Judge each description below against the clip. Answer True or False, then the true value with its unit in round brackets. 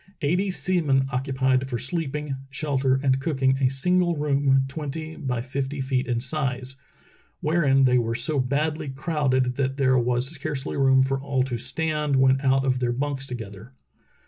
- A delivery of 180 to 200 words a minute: False (165 wpm)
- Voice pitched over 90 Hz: True (135 Hz)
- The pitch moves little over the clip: True (2.2 semitones)